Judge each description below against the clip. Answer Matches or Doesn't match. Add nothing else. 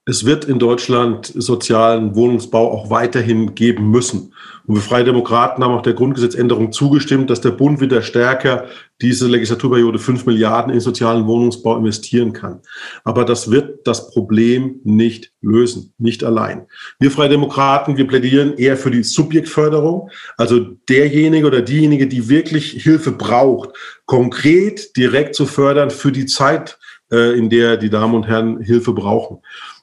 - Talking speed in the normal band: Matches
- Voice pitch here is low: Matches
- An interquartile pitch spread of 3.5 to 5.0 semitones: Doesn't match